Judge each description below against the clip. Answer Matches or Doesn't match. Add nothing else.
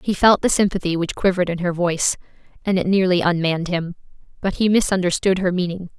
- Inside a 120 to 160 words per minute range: Doesn't match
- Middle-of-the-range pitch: Matches